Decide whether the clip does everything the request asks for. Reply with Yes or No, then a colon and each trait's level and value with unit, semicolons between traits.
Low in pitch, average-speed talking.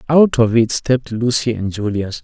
Yes: low, 115 Hz; average, 190 wpm